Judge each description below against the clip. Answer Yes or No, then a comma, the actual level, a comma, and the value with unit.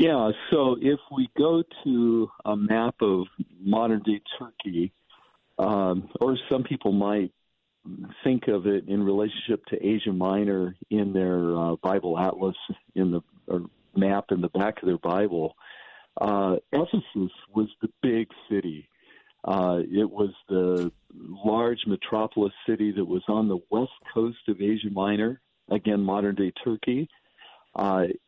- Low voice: Yes, low, 100 Hz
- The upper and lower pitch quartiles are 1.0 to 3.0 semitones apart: Yes, average, 2.7 semitones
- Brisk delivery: No, average, 140 wpm